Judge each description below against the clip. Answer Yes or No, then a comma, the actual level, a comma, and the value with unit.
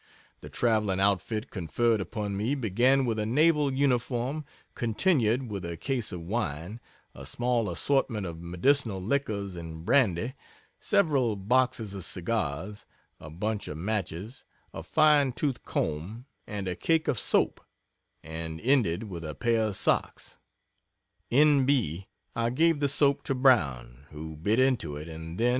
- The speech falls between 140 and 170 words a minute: Yes, average, 150 wpm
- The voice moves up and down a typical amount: No, wide, 6.8 semitones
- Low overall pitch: Yes, low, 110 Hz